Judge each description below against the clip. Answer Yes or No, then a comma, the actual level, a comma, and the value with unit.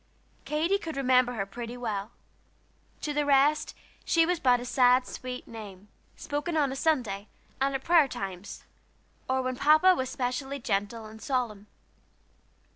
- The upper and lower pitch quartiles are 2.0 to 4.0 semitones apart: No, average, 4.4 semitones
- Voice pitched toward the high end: Yes, very high, 255 Hz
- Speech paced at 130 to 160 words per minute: Yes, average, 145 wpm